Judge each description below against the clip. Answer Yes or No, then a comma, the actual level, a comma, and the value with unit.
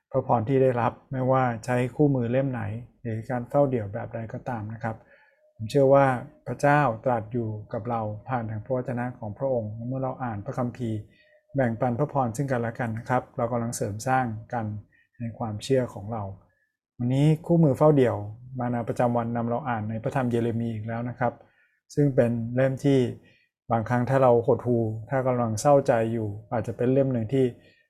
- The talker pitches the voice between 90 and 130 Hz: Yes, low, 120 Hz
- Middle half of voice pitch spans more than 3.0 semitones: No, narrow, 2.5 semitones